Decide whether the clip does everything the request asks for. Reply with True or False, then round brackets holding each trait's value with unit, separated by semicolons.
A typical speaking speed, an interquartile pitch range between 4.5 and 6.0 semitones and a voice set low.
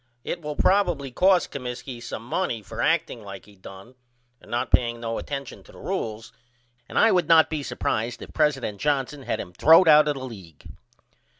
True (190 wpm; 5.1 semitones; 130 Hz)